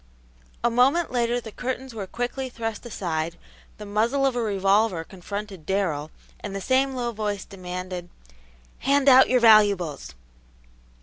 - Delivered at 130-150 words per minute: Yes, average, 140 wpm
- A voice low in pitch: No, high, 215 Hz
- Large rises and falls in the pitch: No, average, 4.4 semitones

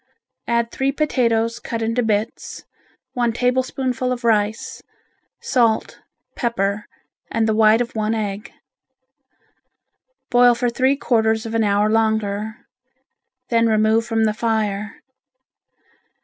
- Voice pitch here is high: Yes, high, 225 Hz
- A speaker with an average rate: No, slow, 115 wpm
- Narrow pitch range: Yes, narrow, 1.8 semitones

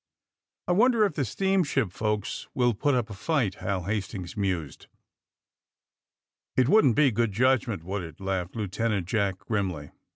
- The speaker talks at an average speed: Yes, average, 150 wpm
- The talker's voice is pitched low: Yes, low, 105 Hz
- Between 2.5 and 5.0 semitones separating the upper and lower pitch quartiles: No, wide, 5.4 semitones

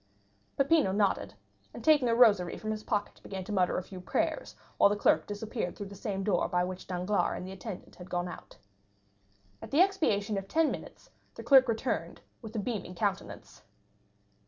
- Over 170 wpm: Yes, average, 185 wpm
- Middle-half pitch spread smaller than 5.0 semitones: Yes, average, 3.6 semitones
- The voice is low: No, high, 205 Hz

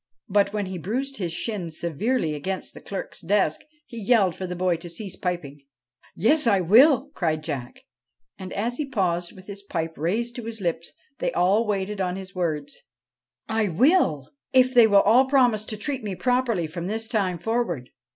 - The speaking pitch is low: No, high, 195 Hz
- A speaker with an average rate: Yes, average, 190 wpm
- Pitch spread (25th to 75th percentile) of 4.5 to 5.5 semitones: Yes, average, 5.0 semitones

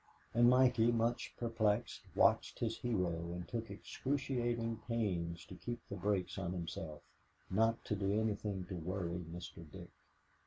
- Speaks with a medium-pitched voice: No, low, 105 Hz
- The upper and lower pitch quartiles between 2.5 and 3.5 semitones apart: No, average, 4.5 semitones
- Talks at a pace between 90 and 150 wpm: Yes, average, 145 wpm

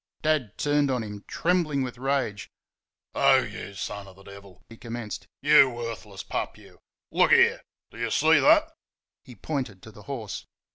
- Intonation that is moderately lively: No, wide, 5.7 semitones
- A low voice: Yes, low, 120 Hz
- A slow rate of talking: No, average, 170 wpm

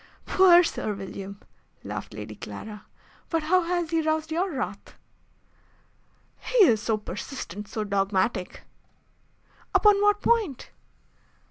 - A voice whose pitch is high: Yes, very high, 310 Hz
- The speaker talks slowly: Yes, slow, 115 wpm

